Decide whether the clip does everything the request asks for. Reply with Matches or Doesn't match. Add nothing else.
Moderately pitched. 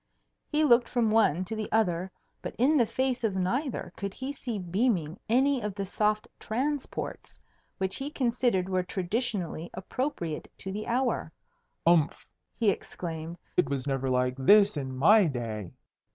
Doesn't match